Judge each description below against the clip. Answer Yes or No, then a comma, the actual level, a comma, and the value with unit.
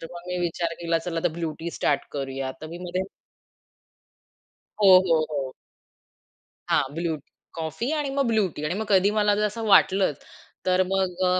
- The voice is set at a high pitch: No, medium, 175 Hz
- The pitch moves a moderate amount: Yes, average, 3.0 semitones